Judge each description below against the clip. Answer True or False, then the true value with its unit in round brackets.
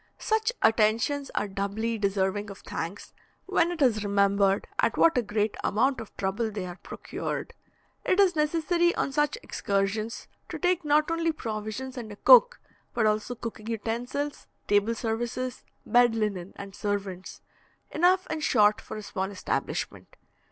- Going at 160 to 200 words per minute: False (150 wpm)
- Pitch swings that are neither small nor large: False (6.4 semitones)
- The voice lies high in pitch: True (225 Hz)